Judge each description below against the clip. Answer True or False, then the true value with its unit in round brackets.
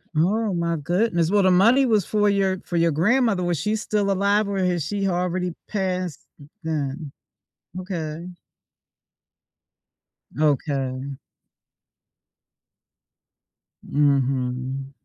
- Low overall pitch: False (180 Hz)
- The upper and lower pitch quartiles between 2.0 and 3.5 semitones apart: False (4.8 semitones)